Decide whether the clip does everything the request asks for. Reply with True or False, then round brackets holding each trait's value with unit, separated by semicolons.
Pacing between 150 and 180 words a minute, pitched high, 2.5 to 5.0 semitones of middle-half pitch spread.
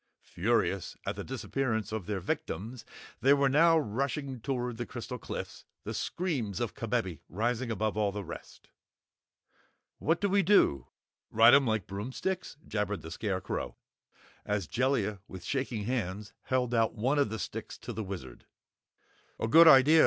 False (155 wpm; 115 Hz; 4.7 semitones)